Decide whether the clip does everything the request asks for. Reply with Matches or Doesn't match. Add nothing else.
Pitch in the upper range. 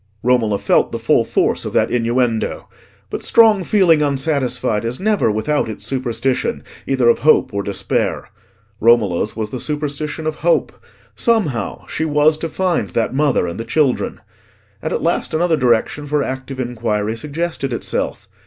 Doesn't match